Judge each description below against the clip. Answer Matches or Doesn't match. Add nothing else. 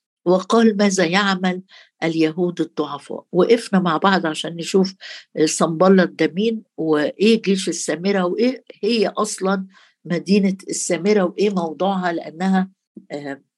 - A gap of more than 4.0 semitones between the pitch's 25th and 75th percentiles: Doesn't match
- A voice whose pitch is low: Doesn't match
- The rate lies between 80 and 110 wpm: Matches